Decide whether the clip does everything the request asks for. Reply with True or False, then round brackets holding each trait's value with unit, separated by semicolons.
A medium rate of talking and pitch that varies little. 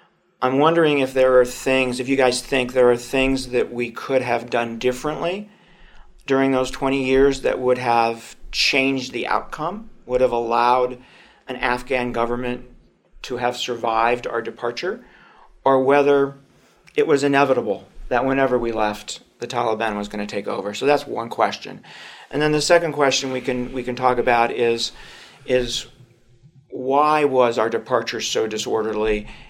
True (160 wpm; 2.1 semitones)